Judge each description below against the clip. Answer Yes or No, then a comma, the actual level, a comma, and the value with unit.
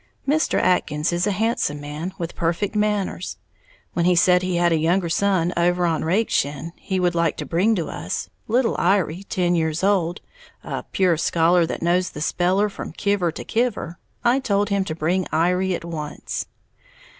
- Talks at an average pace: Yes, average, 175 wpm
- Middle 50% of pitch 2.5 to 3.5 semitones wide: Yes, average, 3.0 semitones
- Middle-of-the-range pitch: Yes, medium, 175 Hz